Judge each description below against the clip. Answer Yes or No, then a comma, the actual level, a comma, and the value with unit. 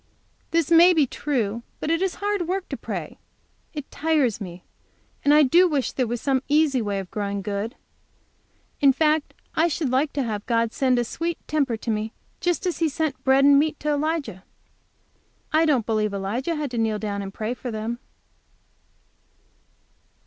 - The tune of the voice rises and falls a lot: Yes, wide, 6.0 semitones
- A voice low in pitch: No, very high, 270 Hz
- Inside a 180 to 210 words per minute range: Yes, average, 185 wpm